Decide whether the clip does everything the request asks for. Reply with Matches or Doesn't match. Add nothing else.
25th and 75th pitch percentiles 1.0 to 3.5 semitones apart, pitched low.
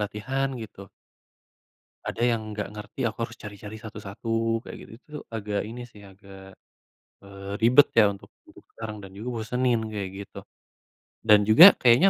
Matches